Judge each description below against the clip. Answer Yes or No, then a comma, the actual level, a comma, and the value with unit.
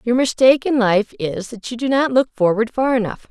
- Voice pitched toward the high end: Yes, high, 235 Hz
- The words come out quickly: Yes, fast, 235 wpm